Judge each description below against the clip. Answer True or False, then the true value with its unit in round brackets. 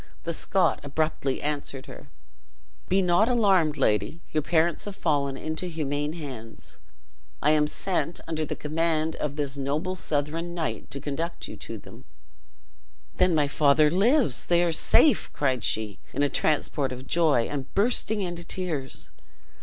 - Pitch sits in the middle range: True (155 Hz)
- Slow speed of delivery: False (155 wpm)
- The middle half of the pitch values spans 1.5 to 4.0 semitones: True (3.4 semitones)